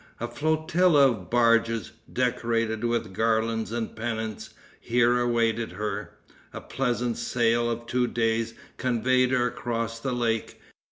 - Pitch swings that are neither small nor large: No, narrow, 1.4 semitones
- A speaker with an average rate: No, slow, 125 wpm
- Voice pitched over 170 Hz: No, low, 115 Hz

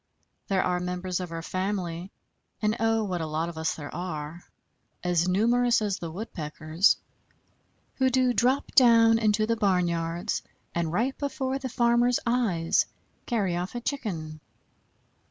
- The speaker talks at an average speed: Yes, average, 145 wpm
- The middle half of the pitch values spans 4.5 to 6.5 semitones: Yes, wide, 5.6 semitones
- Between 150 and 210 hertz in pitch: Yes, high, 190 Hz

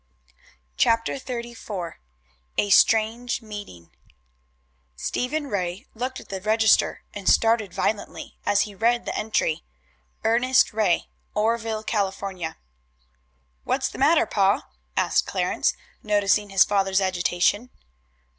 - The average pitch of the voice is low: No, high, 210 Hz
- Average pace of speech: No, slow, 110 wpm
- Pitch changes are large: No, average, 2.9 semitones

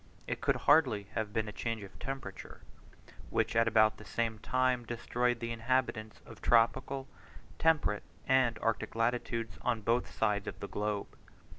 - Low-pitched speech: Yes, low, 115 Hz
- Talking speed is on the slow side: No, average, 155 wpm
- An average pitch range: No, narrow, 2.3 semitones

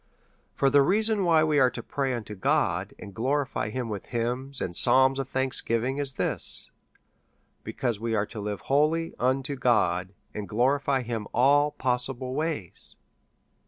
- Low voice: Yes, low, 130 Hz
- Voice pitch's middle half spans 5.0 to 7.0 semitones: No, average, 3.6 semitones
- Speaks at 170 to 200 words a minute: No, average, 160 wpm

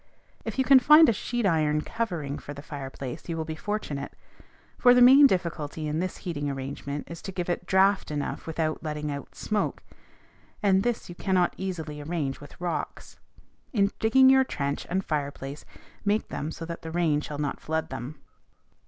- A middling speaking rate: Yes, average, 180 wpm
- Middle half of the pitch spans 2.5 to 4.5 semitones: No, average, 5.2 semitones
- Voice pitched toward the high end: No, medium, 165 Hz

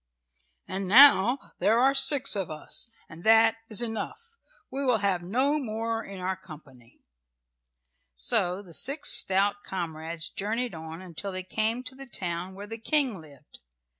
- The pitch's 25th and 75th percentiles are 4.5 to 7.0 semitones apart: Yes, average, 5.2 semitones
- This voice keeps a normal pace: Yes, average, 155 wpm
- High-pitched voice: Yes, high, 200 Hz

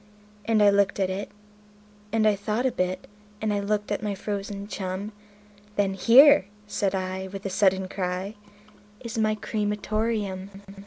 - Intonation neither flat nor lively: No, narrow, 1.9 semitones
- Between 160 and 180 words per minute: Yes, average, 170 wpm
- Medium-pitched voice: No, high, 200 Hz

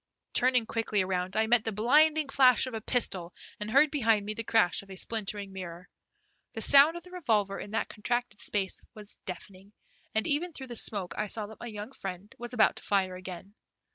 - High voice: Yes, high, 215 Hz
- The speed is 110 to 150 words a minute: No, fast, 205 wpm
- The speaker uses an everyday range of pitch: Yes, average, 4.1 semitones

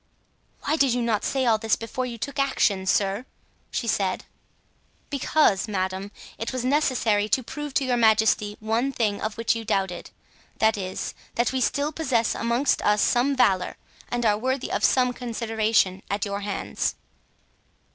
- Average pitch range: Yes, average, 3.8 semitones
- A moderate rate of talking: Yes, average, 165 wpm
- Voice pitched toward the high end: Yes, high, 230 Hz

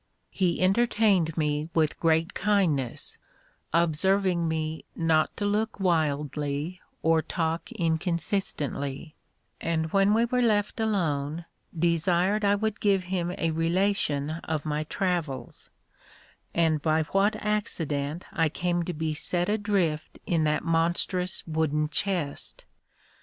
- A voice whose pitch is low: No, medium, 170 Hz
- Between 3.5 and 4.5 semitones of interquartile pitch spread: Yes, average, 3.8 semitones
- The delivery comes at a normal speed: No, slow, 120 wpm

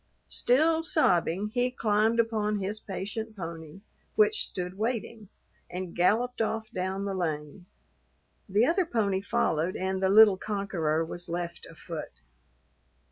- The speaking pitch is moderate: No, high, 200 Hz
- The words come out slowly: Yes, slow, 130 wpm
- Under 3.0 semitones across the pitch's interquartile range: No, average, 3.9 semitones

